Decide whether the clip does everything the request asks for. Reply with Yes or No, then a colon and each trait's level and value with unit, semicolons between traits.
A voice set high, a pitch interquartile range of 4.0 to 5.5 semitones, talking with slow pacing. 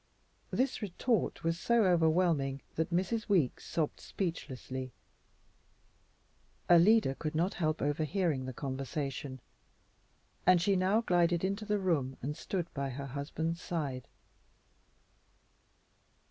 No: medium, 165 Hz; average, 5.0 semitones; slow, 110 wpm